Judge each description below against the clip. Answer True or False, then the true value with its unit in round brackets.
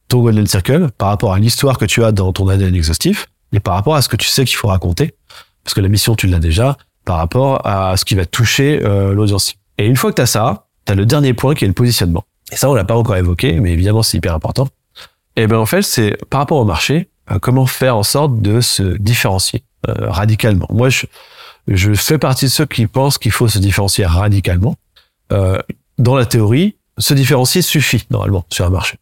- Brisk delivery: True (225 wpm)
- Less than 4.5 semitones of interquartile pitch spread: False (4.8 semitones)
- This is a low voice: True (110 Hz)